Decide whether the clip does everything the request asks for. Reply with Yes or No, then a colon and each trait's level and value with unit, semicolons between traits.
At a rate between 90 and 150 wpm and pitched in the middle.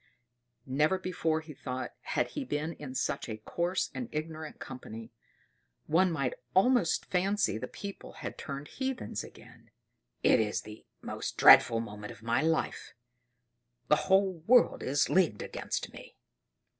Yes: average, 145 wpm; medium, 155 Hz